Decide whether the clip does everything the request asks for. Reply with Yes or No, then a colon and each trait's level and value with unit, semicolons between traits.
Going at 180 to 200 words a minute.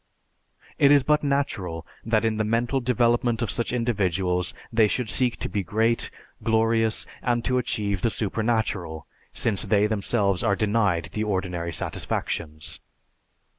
No: average, 140 wpm